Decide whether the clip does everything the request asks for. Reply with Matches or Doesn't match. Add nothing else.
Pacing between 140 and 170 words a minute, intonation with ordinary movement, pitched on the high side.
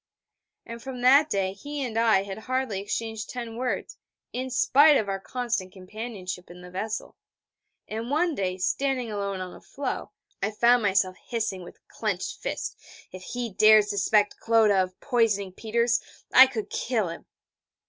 Matches